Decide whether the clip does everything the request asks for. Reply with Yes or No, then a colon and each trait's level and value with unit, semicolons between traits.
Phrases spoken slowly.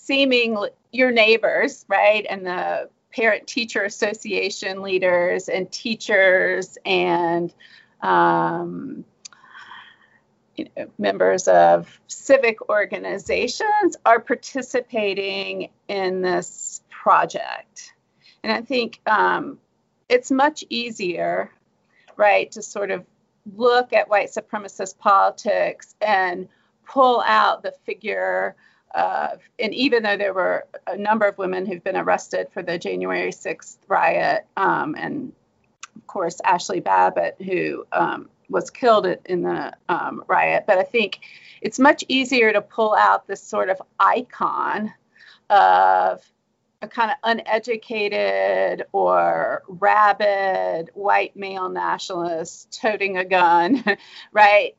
Yes: slow, 115 wpm